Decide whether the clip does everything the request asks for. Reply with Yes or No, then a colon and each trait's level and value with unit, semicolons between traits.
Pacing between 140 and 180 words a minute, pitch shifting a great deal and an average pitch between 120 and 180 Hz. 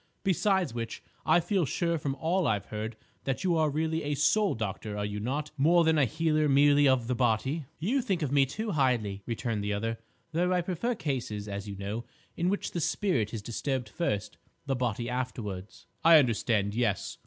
No: average, 195 wpm; wide, 6.7 semitones; low, 135 Hz